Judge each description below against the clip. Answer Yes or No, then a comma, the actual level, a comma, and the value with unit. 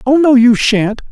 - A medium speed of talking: No, fast, 215 wpm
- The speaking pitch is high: Yes, very high, 250 Hz